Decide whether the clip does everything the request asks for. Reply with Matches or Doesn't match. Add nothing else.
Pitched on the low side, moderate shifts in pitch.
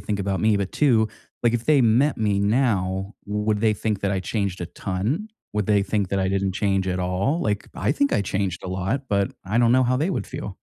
Matches